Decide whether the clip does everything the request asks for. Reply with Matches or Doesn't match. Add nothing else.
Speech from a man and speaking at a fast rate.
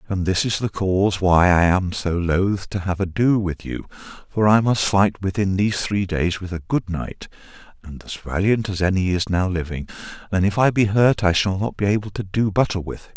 Matches